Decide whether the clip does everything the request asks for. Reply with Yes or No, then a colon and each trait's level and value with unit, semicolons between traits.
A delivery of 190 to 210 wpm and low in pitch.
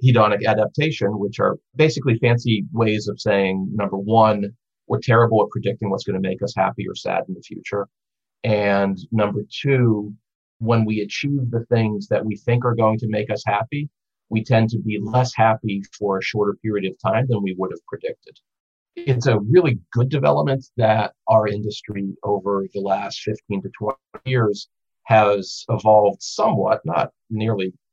No: average, 170 wpm; low, 110 Hz